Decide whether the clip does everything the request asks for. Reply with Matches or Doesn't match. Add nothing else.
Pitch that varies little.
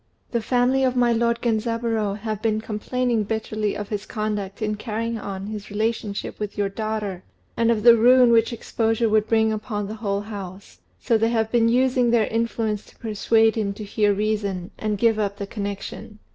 Matches